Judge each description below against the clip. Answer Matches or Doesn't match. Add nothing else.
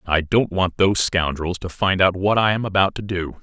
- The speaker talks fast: Matches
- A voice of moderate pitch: Doesn't match